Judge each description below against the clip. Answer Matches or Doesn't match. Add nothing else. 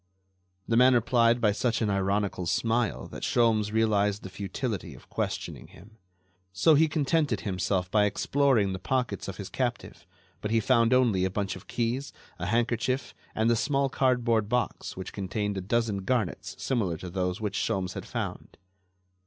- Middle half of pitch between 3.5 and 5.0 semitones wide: Matches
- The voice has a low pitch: Matches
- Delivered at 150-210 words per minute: Matches